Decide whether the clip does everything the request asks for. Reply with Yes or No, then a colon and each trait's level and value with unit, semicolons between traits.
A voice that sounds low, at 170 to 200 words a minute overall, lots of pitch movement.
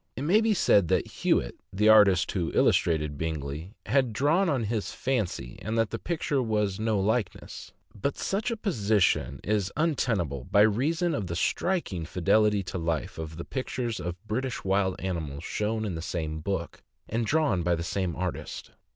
Yes: low, 105 Hz; average, 175 wpm; wide, 6.3 semitones